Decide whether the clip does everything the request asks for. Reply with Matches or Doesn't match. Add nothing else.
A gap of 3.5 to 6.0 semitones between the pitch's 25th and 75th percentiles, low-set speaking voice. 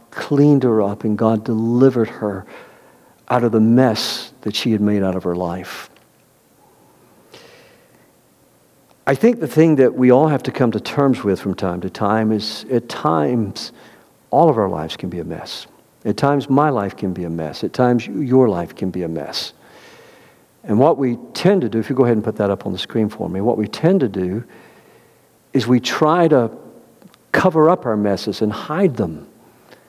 Matches